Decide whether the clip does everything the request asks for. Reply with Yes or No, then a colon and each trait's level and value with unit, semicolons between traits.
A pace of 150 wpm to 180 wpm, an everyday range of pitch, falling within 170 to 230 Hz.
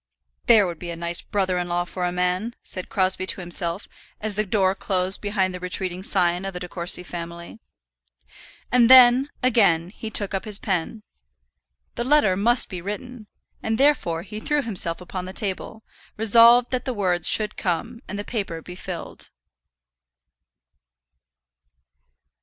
Yes: average, 160 wpm; average, 3.7 semitones; high, 190 Hz